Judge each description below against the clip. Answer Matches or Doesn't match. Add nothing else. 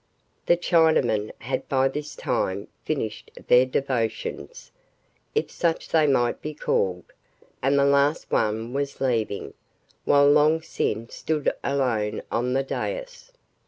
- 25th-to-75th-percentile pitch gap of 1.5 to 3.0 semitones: Doesn't match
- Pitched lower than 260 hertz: Matches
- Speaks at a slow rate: Matches